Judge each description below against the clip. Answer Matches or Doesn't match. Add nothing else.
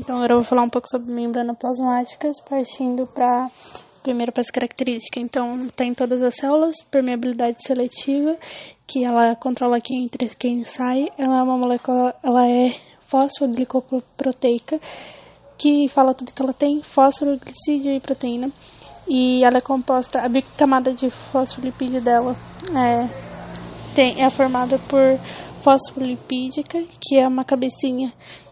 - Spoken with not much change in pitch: Matches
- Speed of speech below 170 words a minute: Matches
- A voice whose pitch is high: Matches